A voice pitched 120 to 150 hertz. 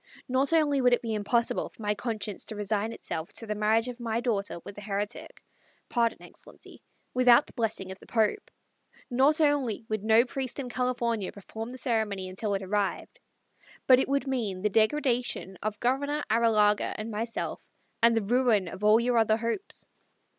No: high, 225 Hz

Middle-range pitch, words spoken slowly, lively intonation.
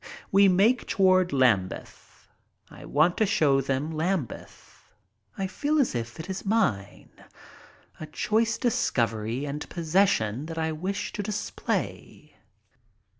Yes: medium, 165 Hz; slow, 125 wpm; wide, 6.5 semitones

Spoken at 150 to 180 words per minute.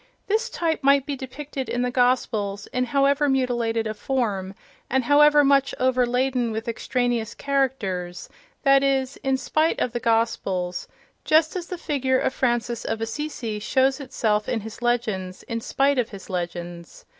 Yes: average, 155 wpm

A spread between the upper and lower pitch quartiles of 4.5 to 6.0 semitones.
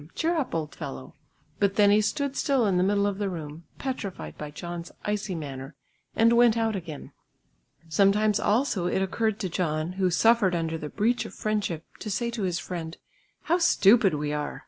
Yes: average, 5.0 semitones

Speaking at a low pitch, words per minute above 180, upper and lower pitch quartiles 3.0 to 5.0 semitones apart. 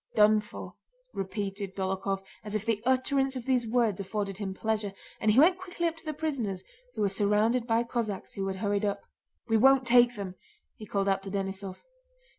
No: high, 210 Hz; average, 195 wpm; average, 3.7 semitones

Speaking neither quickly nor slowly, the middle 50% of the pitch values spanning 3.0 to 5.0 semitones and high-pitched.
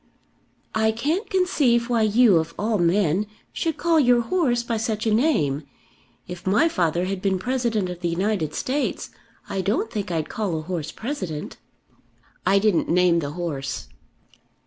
No: average, 160 wpm; wide, 5.6 semitones; high, 205 Hz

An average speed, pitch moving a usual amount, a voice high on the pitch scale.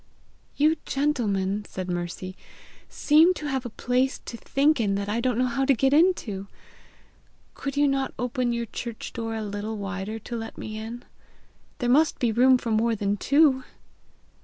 Yes: average, 175 wpm; average, 4.2 semitones; high, 235 Hz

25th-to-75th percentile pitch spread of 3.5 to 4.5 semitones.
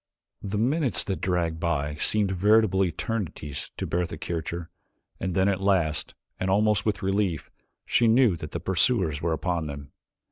Yes: average, 3.9 semitones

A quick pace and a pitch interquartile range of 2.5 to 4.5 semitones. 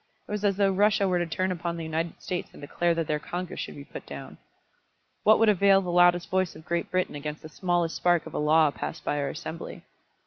Yes: fast, 240 wpm; average, 2.8 semitones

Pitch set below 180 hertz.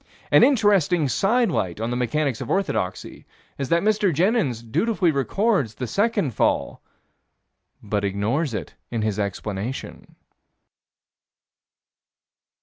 Yes: medium, 140 Hz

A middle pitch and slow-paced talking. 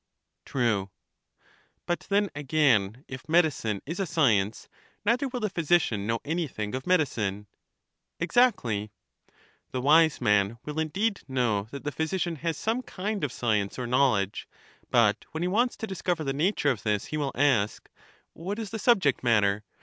No: medium, 145 Hz; average, 155 wpm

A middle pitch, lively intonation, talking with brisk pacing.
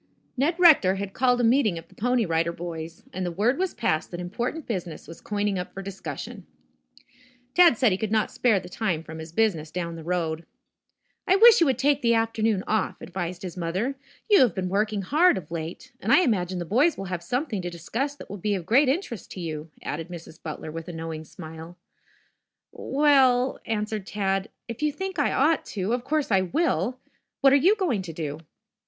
No: high, 200 Hz; wide, 6.9 semitones; fast, 215 wpm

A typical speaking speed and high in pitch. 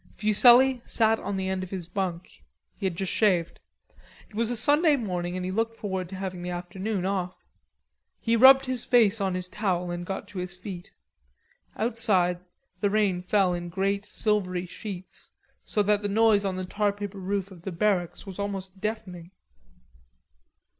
Yes: average, 175 wpm; high, 195 Hz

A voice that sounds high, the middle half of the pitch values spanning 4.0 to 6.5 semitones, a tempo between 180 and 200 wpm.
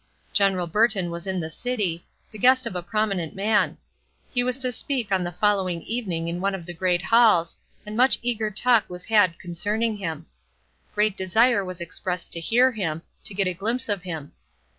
Yes: high, 195 Hz; average, 4.3 semitones; average, 190 wpm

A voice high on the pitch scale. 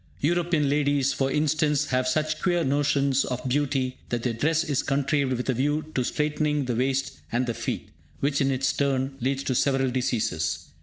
No: medium, 140 Hz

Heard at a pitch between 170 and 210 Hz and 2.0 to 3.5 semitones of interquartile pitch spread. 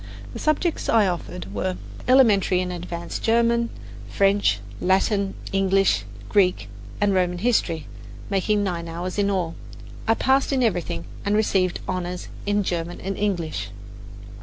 Yes: high, 190 Hz; average, 3.1 semitones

